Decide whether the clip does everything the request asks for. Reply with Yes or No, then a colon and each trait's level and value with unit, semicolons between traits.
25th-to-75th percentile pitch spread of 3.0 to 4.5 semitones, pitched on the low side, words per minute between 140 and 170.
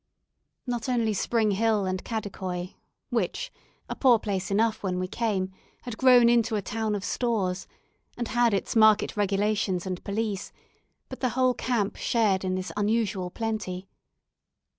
No: average, 3.3 semitones; high, 215 Hz; average, 150 wpm